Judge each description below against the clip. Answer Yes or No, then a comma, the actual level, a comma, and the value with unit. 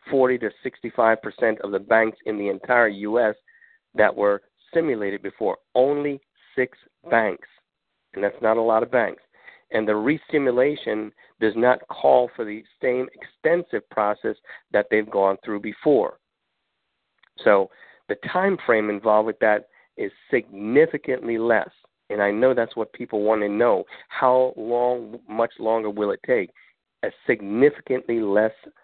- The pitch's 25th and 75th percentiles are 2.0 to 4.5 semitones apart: Yes, average, 3.2 semitones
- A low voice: Yes, low, 115 Hz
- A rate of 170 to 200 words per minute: No, average, 145 wpm